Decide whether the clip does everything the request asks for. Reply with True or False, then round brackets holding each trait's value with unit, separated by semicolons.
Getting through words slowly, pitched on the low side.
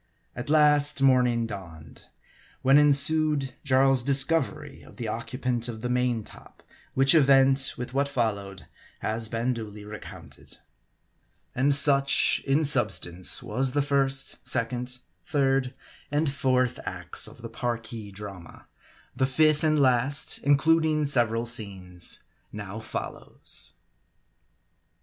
True (120 wpm; 130 Hz)